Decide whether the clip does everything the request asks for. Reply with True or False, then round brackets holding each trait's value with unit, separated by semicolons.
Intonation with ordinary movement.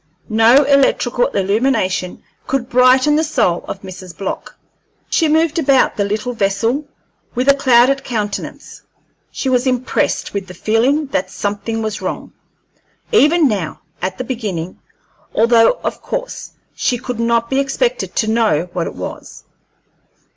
True (5.0 semitones)